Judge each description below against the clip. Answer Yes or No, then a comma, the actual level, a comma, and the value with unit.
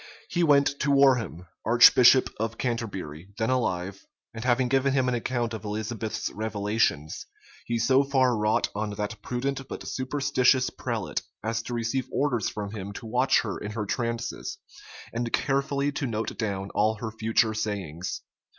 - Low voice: Yes, low, 115 Hz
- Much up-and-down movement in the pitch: No, average, 3.6 semitones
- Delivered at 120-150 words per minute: No, average, 160 wpm